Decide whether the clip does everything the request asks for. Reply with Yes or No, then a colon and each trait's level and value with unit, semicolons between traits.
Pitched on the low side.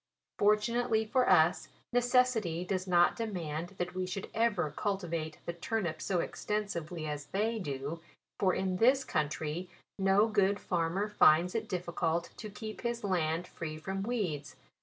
No: medium, 185 Hz